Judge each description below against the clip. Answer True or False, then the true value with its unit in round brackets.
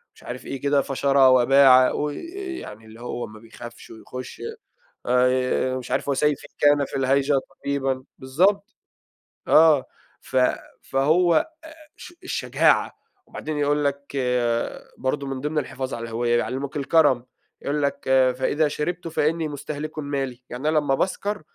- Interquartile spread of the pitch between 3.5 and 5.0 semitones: False (2.6 semitones)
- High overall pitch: False (140 Hz)